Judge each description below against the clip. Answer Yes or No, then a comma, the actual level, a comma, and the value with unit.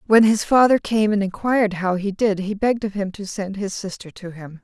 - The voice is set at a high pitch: Yes, high, 205 Hz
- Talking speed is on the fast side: Yes, fast, 245 wpm